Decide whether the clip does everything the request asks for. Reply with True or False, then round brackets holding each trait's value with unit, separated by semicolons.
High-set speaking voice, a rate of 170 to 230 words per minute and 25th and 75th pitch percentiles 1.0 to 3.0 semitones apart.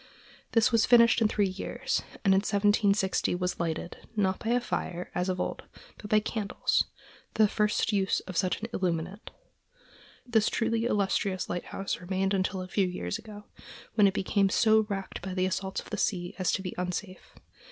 True (195 Hz; 175 wpm; 2.4 semitones)